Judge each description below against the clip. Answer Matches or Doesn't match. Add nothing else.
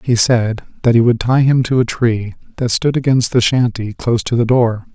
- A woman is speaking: Doesn't match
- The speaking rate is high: Matches